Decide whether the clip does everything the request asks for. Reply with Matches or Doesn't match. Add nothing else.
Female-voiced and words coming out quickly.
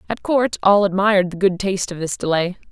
Matches